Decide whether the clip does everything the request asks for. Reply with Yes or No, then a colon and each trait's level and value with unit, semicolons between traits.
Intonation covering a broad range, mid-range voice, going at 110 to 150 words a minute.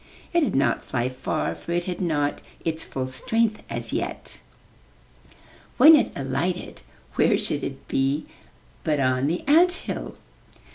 Yes: wide, 8.7 semitones; medium, 160 Hz; average, 145 wpm